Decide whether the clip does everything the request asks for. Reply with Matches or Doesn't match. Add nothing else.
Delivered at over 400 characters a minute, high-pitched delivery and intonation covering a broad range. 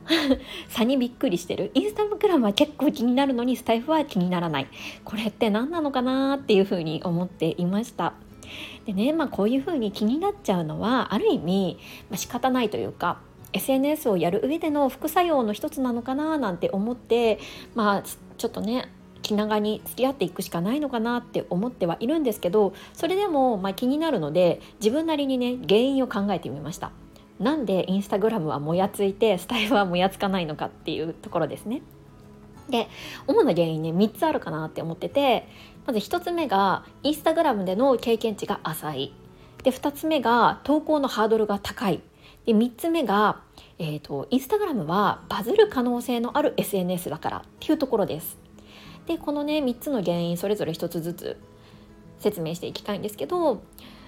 Doesn't match